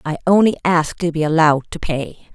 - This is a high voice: No, medium, 165 Hz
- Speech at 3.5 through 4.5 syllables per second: No, 6.0 syllables/s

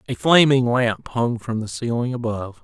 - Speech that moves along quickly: No, average, 180 wpm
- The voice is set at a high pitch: No, low, 120 Hz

